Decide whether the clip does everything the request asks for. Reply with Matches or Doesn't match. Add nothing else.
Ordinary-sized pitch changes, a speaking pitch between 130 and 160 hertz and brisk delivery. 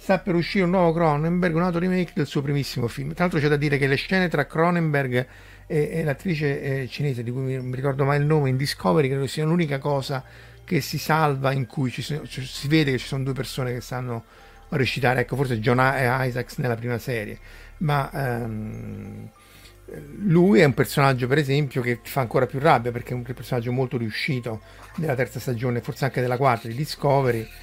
Matches